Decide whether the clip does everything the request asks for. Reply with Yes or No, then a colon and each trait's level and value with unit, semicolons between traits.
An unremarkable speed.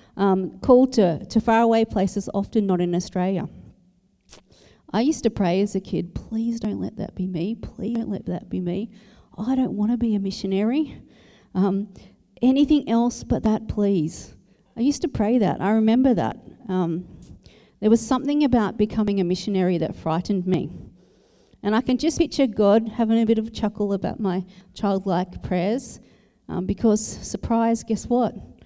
Yes: average, 175 wpm